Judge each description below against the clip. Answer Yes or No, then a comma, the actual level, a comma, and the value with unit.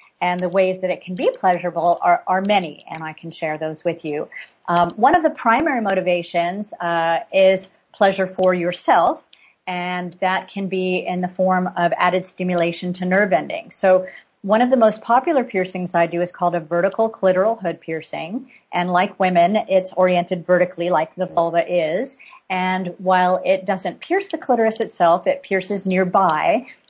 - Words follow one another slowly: No, average, 175 wpm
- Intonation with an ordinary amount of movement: No, narrow, 1.9 semitones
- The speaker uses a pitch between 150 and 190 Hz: Yes, medium, 185 Hz